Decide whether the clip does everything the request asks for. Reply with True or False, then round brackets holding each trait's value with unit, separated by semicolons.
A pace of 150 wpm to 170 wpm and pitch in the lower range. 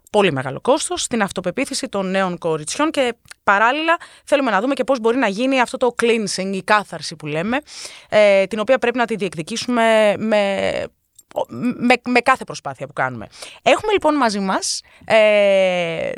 False (165 wpm; 220 Hz)